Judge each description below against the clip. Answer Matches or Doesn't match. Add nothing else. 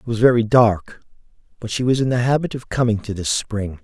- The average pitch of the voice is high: Doesn't match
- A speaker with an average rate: Doesn't match